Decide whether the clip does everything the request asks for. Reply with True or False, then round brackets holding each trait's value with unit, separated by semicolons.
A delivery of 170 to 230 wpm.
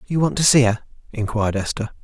True (205 wpm)